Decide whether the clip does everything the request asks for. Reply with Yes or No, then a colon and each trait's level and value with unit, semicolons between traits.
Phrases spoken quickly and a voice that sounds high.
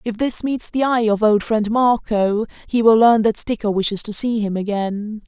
Yes: fast, 215 wpm; high, 220 Hz